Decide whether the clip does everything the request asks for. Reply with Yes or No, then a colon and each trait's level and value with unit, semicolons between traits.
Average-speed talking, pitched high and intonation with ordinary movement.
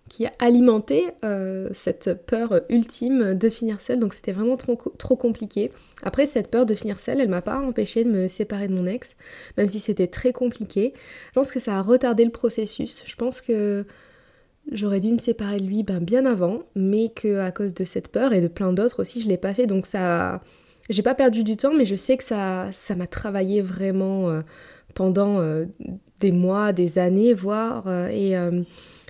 Yes: average, 210 wpm; high, 210 Hz; average, 3.8 semitones